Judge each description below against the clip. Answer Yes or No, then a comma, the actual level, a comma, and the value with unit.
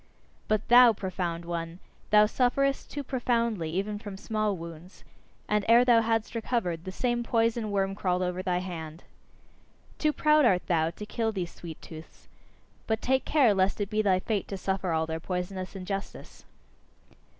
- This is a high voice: Yes, high, 200 Hz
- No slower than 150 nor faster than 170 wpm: Yes, average, 165 wpm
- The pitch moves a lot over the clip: No, average, 4.2 semitones